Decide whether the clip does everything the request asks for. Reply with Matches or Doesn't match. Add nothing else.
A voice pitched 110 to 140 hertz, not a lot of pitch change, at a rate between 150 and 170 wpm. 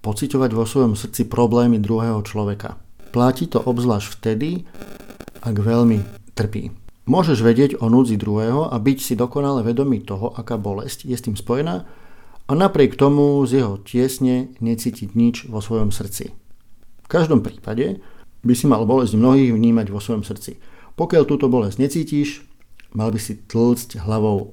Doesn't match